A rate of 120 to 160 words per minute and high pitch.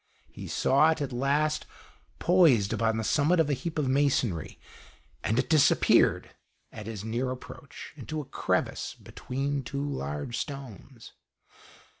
No: average, 140 wpm; low, 135 Hz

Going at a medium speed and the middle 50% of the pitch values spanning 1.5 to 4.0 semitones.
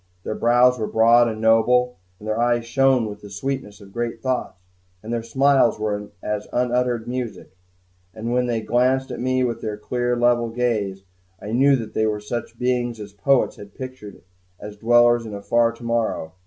Yes: average, 185 wpm; narrow, 2.4 semitones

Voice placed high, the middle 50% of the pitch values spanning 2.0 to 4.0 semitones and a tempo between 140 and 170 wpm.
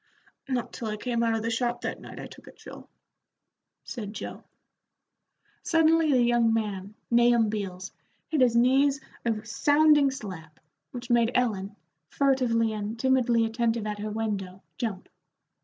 Yes: high, 230 Hz; average, 2.8 semitones; average, 150 wpm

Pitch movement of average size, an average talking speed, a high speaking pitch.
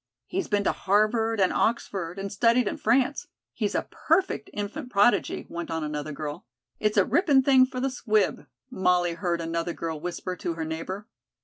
No: wide, 6.1 semitones; average, 180 wpm; high, 200 Hz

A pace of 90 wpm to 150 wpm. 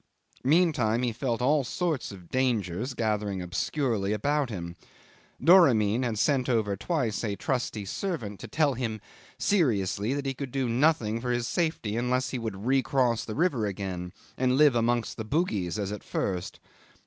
No: average, 160 wpm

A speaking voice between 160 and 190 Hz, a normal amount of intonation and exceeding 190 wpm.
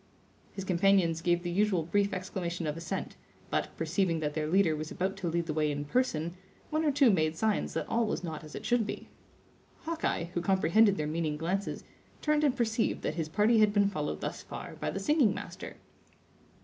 Yes: medium, 185 Hz; average, 4.6 semitones; average, 200 wpm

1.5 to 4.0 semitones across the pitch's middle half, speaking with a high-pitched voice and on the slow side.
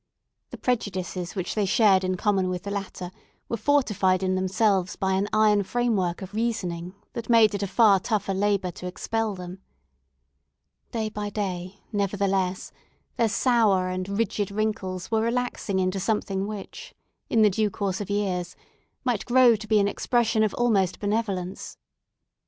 No: average, 2.7 semitones; high, 200 Hz; average, 160 wpm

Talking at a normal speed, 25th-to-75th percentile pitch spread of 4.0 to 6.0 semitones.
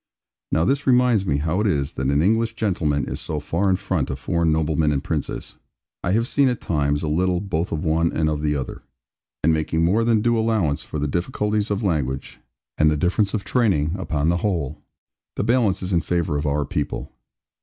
No: fast, 210 wpm; wide, 5.6 semitones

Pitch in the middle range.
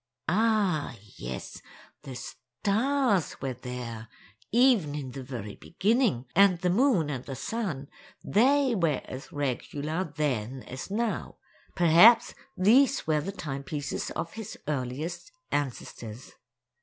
Yes: medium, 155 Hz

